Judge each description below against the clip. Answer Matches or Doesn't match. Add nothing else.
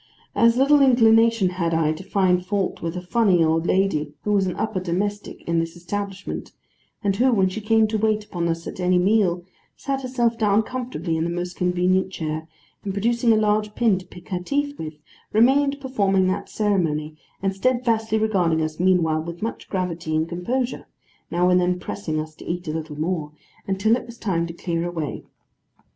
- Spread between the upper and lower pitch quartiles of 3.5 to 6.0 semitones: Matches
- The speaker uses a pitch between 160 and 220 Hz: Matches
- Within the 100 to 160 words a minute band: Doesn't match